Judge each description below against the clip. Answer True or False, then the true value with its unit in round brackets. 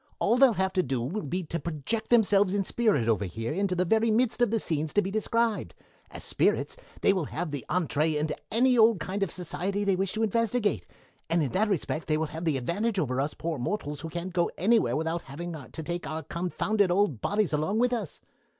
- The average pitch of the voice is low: False (180 Hz)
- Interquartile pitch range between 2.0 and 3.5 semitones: False (5.3 semitones)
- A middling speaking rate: False (225 wpm)